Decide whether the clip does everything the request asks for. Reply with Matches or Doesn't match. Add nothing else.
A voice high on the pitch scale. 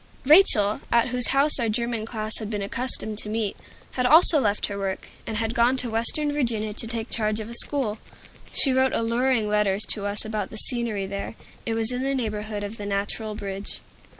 Matches